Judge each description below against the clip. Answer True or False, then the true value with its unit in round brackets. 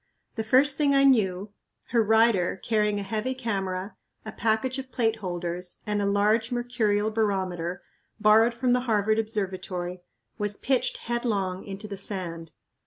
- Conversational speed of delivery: True (150 wpm)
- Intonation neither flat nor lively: True (3.3 semitones)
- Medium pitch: False (210 Hz)